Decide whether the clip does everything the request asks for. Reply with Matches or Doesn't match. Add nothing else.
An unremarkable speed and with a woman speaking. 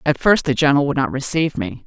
Doesn't match